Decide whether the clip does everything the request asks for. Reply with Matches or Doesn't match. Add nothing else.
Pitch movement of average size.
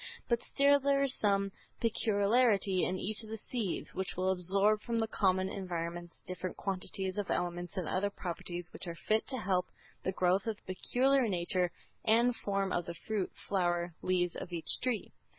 Matches